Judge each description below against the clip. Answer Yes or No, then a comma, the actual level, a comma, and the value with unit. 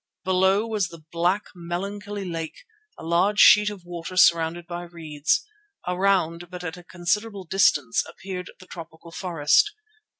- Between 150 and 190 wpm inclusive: No, average, 140 wpm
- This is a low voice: No, medium, 180 Hz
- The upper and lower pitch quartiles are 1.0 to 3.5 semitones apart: Yes, average, 2.7 semitones